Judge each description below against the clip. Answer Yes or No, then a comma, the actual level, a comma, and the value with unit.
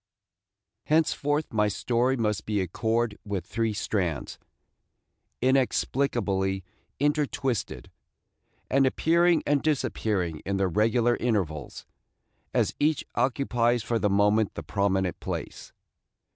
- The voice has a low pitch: Yes, low, 115 Hz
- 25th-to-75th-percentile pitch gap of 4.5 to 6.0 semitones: Yes, average, 5.1 semitones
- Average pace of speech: No, slow, 105 wpm